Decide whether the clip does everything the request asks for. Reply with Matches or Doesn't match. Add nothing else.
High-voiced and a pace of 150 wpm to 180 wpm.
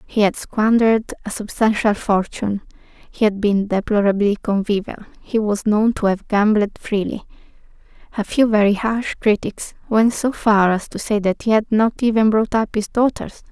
Matches